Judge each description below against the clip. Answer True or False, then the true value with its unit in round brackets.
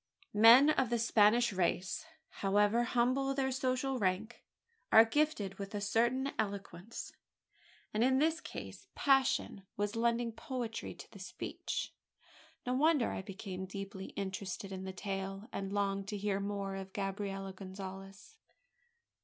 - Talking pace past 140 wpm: False (135 wpm)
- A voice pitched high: True (205 Hz)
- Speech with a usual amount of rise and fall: True (4.0 semitones)